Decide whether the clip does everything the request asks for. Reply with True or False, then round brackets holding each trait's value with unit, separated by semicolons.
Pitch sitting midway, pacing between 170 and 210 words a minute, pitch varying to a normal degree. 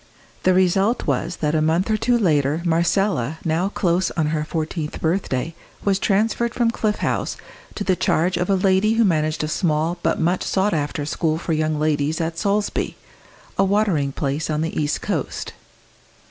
True (170 Hz; 175 wpm; 4.0 semitones)